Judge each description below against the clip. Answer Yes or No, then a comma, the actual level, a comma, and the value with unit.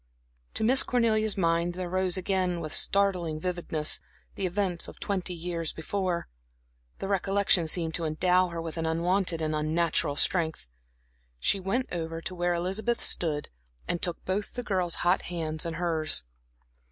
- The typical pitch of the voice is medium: Yes, medium, 175 Hz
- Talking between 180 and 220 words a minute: No, average, 155 wpm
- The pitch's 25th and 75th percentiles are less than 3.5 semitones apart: Yes, narrow, 2.6 semitones